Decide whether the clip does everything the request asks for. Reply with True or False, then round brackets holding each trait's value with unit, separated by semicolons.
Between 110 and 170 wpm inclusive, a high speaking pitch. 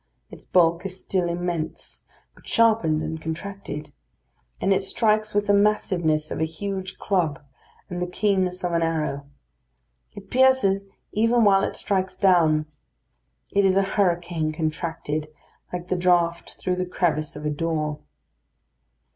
False (145 wpm; 180 Hz)